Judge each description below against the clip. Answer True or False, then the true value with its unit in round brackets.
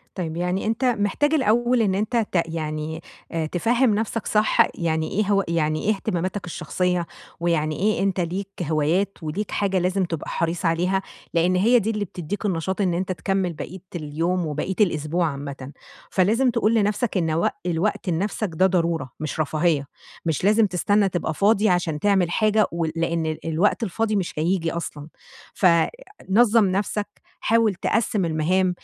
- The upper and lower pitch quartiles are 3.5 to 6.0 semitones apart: True (4.0 semitones)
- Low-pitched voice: False (180 Hz)